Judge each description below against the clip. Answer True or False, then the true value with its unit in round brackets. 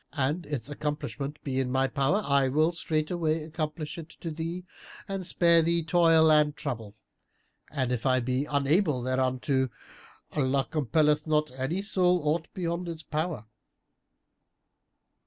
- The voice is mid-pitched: True (150 Hz)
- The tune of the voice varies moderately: True (3.7 semitones)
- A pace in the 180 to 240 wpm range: False (140 wpm)